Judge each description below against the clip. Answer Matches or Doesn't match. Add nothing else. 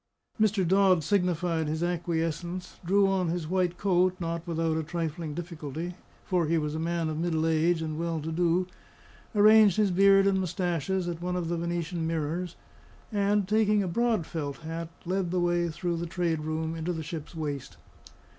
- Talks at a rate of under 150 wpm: Doesn't match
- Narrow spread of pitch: Matches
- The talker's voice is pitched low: Doesn't match